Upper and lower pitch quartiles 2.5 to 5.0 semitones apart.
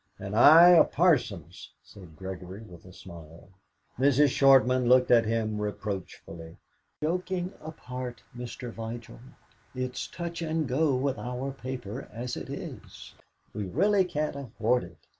No: wide, 5.4 semitones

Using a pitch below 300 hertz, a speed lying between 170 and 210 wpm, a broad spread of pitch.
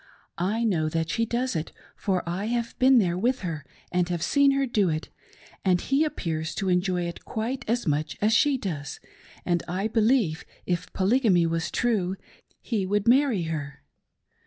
Yes: high, 190 Hz; average, 175 wpm; wide, 5.7 semitones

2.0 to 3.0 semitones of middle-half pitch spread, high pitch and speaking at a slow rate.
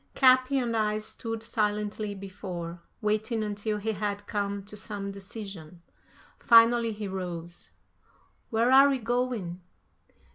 Yes: narrow, 2.6 semitones; high, 210 Hz; slow, 120 wpm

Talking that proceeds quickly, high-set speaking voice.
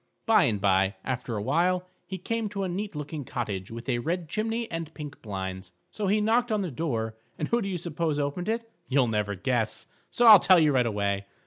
No: fast, 220 wpm; medium, 150 Hz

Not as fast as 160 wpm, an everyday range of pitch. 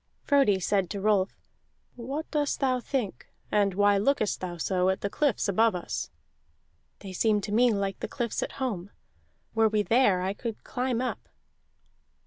No: average, 165 wpm; average, 4.2 semitones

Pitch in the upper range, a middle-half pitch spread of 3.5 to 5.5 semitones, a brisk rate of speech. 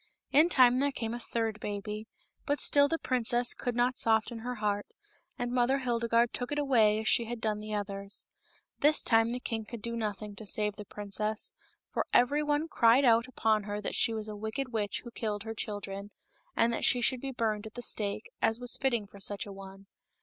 No: high, 225 Hz; average, 2.8 semitones; fast, 215 wpm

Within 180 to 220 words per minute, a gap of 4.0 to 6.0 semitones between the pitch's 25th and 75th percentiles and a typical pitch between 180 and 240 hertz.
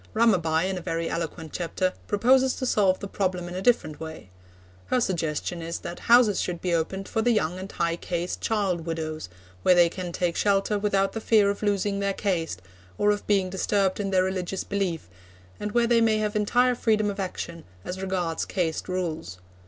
No: average, 195 wpm; average, 3.4 semitones; high, 190 Hz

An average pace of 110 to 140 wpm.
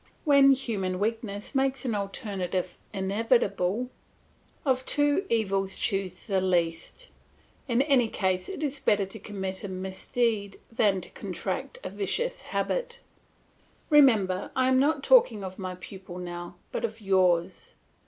Yes: slow, 135 wpm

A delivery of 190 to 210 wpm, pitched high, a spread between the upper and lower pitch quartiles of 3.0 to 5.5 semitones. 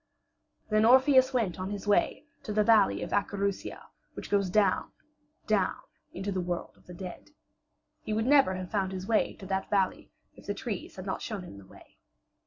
No: average, 195 wpm; high, 200 Hz; narrow, 2.6 semitones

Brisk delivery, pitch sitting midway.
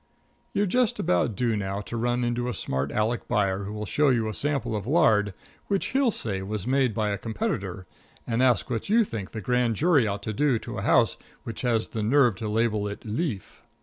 No: fast, 215 wpm; low, 115 Hz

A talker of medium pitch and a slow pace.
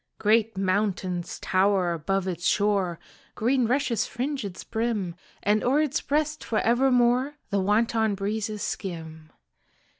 No: high, 210 Hz; slow, 125 wpm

